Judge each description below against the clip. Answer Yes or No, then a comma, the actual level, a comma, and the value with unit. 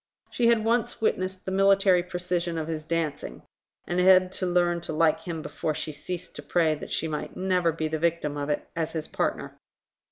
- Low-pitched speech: No, medium, 170 Hz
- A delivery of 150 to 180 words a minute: No, average, 200 wpm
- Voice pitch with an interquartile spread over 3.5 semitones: No, average, 2.7 semitones